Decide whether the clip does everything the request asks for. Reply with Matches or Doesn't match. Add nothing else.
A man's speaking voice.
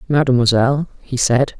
Doesn't match